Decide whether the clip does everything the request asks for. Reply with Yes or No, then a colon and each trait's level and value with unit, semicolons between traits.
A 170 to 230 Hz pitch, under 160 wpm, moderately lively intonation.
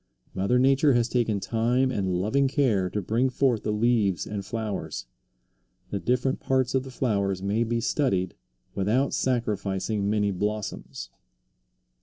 No: low, 110 Hz; average, 140 wpm; average, 4.1 semitones